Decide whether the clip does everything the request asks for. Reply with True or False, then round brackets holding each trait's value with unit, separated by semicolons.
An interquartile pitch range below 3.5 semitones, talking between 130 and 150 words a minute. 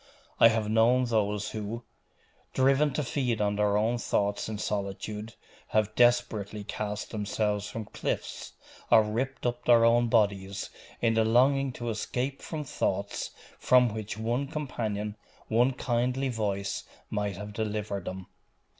True (2.8 semitones; 140 wpm)